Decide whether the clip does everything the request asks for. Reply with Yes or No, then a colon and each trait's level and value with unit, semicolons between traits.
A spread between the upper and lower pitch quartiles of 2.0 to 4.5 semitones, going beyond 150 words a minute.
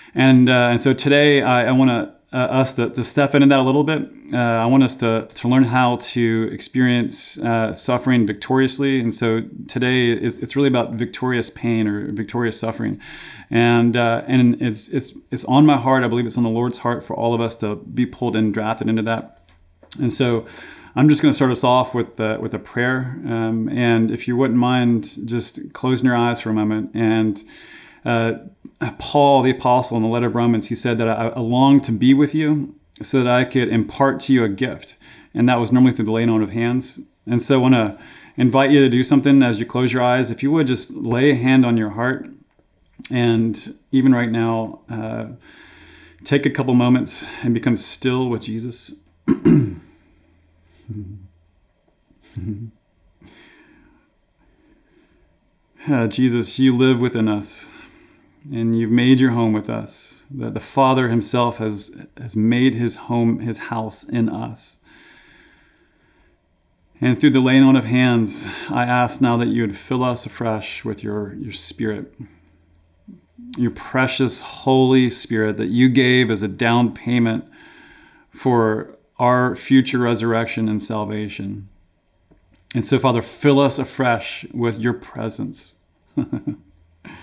Yes: narrow, 2.6 semitones; average, 170 wpm